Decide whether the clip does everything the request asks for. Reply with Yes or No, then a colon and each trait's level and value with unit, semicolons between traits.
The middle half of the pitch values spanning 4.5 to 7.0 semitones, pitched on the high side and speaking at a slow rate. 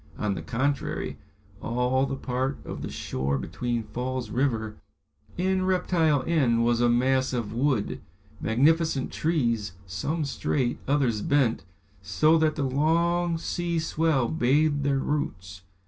No: average, 4.9 semitones; low, 135 Hz; slow, 130 wpm